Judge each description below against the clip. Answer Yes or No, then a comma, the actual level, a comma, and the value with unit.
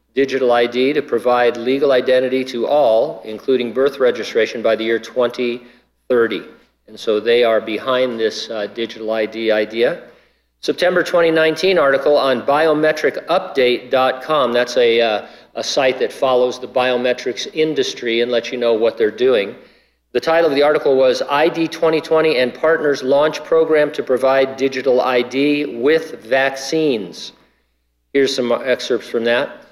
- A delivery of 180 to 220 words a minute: No, average, 140 wpm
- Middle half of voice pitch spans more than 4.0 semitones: Yes, average, 4.5 semitones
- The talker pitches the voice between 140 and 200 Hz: No, low, 130 Hz